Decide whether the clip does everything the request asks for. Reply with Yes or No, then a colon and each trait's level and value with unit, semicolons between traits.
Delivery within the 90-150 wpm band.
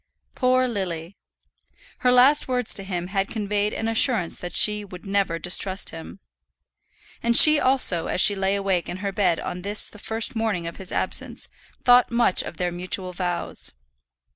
No: average, 170 wpm